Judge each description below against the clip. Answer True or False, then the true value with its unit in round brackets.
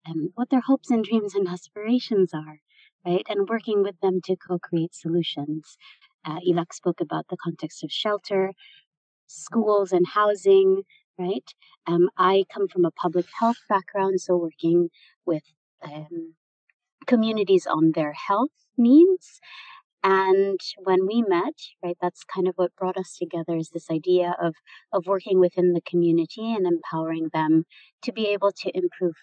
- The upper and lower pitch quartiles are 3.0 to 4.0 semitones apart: True (3.7 semitones)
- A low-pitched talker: False (185 Hz)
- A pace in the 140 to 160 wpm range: True (155 wpm)